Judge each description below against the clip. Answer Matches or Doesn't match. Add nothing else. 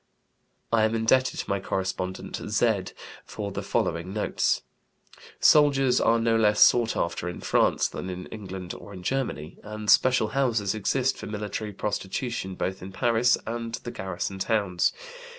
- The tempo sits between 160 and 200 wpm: Doesn't match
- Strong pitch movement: Doesn't match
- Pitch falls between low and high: Doesn't match